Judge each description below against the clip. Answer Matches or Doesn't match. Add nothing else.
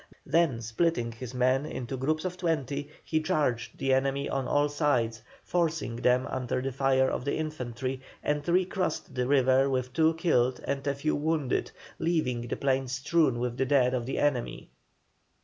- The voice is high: Doesn't match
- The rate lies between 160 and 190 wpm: Matches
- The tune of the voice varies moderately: Matches